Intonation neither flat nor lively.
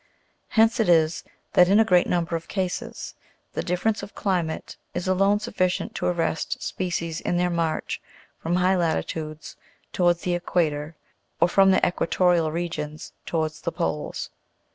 No: narrow, 2.2 semitones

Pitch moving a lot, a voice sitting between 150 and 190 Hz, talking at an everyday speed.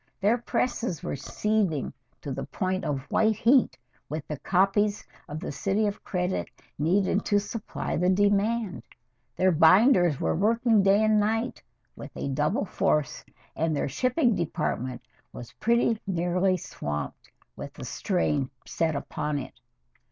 Yes: wide, 5.9 semitones; medium, 185 Hz; average, 145 wpm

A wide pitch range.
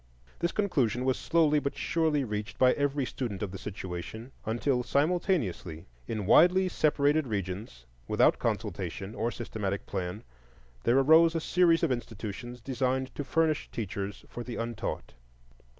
Yes: wide, 6.3 semitones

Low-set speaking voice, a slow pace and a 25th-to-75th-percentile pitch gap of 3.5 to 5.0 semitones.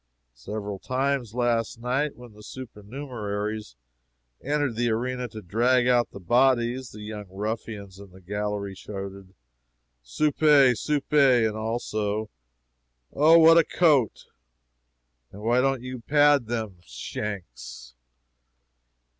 Yes: low, 115 Hz; slow, 115 wpm; average, 3.9 semitones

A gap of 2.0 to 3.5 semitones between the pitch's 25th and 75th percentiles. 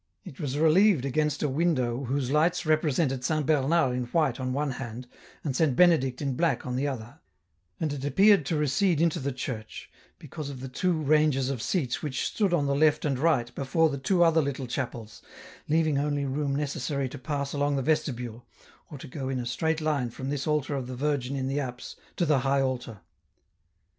Yes: average, 3.1 semitones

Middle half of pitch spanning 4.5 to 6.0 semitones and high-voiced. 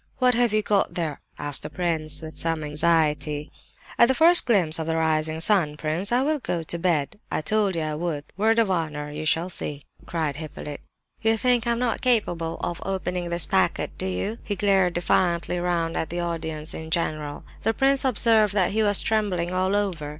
No: average, 5.0 semitones; medium, 175 Hz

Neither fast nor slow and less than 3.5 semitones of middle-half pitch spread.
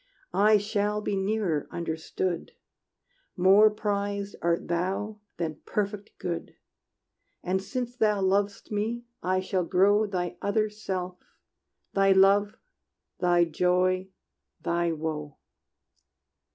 No: slow, 105 wpm; average, 2.7 semitones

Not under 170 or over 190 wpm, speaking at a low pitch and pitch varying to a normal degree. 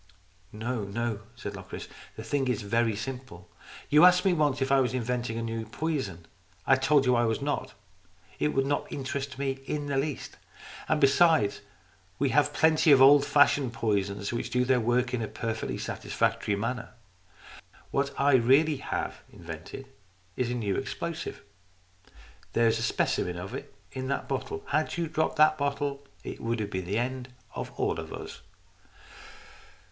Yes: average, 175 wpm; low, 130 Hz; average, 3.9 semitones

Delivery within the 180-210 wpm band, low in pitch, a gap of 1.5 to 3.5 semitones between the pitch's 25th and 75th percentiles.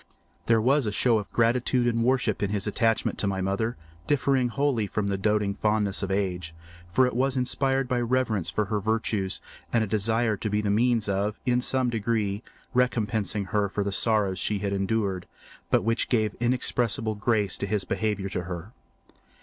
Yes: average, 185 wpm; low, 110 Hz; average, 3.2 semitones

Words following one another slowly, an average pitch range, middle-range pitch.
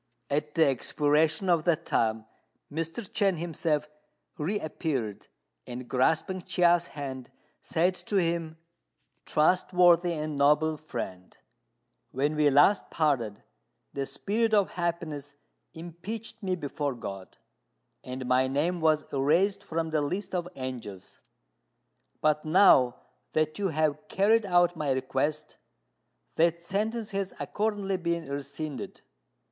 Yes: slow, 120 wpm; average, 4.1 semitones; medium, 155 Hz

